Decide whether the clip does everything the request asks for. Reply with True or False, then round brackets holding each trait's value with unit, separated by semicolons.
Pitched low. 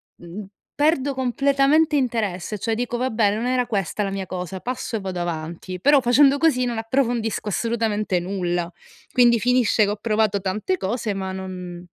False (220 Hz)